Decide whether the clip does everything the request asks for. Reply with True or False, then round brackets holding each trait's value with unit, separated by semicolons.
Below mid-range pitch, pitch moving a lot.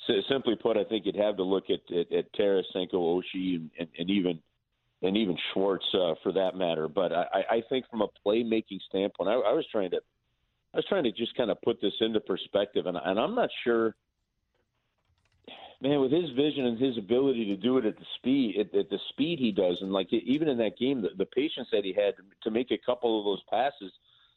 True (115 Hz; 6.8 semitones)